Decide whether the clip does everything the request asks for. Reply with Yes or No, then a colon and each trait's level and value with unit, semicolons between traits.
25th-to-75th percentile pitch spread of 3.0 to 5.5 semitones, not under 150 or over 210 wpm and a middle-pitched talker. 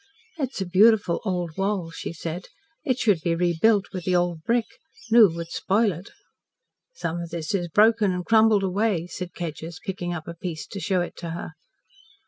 Yes: average, 3.5 semitones; average, 185 wpm; medium, 180 Hz